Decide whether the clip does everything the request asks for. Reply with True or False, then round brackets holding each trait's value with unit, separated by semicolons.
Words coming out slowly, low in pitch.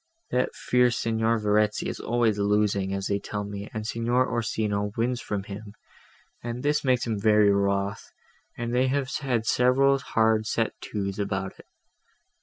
False (160 wpm; 110 Hz)